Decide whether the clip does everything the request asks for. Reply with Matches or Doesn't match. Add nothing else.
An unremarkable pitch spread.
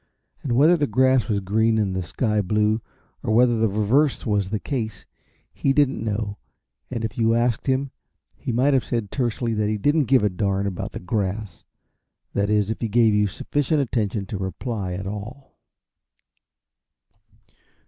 Matches